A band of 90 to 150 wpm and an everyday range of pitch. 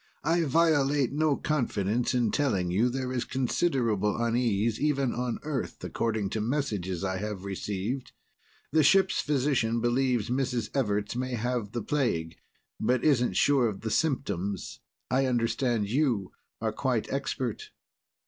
Yes: average, 140 wpm; average, 4.4 semitones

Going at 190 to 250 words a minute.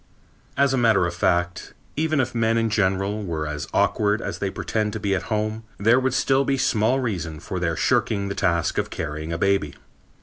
Yes: fast, 205 wpm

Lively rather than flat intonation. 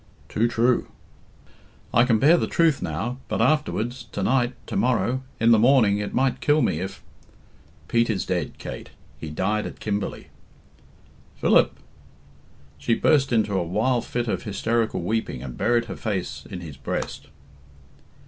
No: average, 3.8 semitones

